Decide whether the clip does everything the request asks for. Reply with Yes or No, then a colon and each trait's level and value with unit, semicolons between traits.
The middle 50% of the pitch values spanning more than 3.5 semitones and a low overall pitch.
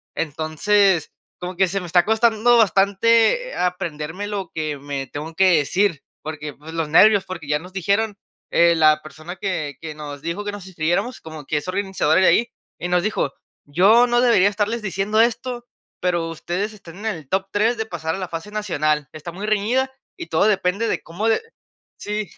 No: average, 4.8 semitones; medium, 185 Hz